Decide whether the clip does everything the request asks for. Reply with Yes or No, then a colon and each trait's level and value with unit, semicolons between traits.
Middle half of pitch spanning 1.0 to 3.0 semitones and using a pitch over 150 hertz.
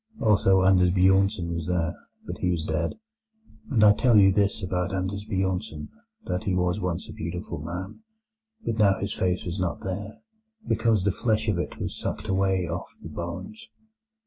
No: narrow, 2.5 semitones; very low, 95 Hz